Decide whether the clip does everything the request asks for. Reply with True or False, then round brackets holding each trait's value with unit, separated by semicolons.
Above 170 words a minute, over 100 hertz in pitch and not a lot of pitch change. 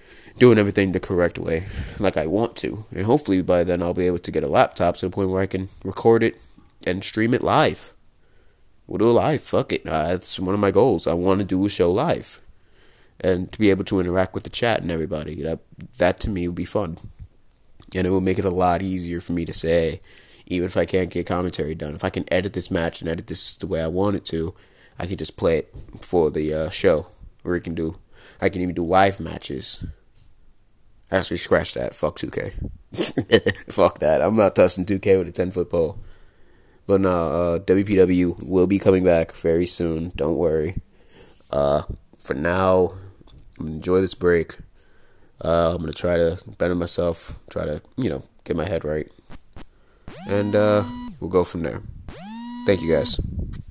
False (205 wpm; 90 Hz; 2.3 semitones)